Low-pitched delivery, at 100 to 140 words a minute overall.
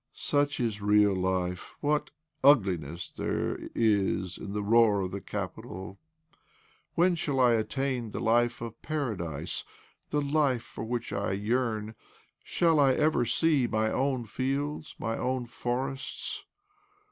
Yes: low, 120 Hz; slow, 135 wpm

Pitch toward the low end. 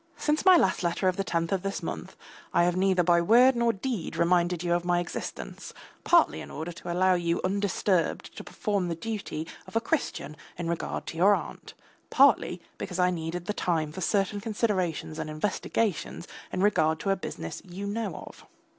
No: medium, 180 Hz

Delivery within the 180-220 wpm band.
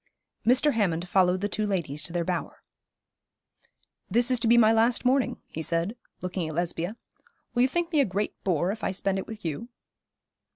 Yes: average, 195 wpm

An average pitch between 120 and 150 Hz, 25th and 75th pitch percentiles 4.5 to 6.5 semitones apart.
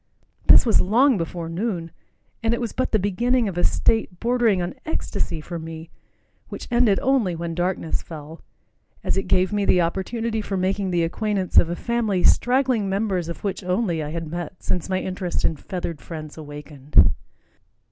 No: medium, 185 Hz; average, 4.8 semitones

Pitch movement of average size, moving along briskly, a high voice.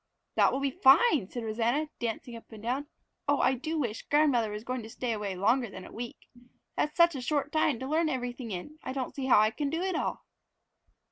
Yes: average, 4.4 semitones; fast, 225 wpm; very high, 255 Hz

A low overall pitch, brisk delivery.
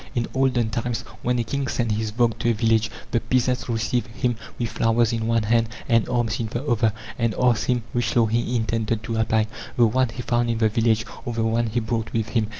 Yes: low, 115 Hz; fast, 235 wpm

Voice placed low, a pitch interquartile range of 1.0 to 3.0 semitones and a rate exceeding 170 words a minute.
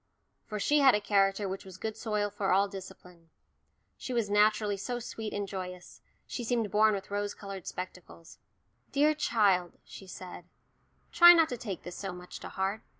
No: high, 205 Hz; narrow, 2.5 semitones; average, 180 wpm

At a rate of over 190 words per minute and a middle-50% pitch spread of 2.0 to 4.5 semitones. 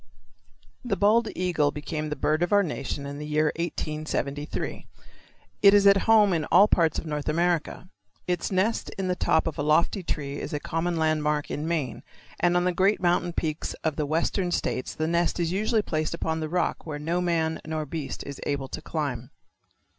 Yes: average, 200 wpm; average, 2.9 semitones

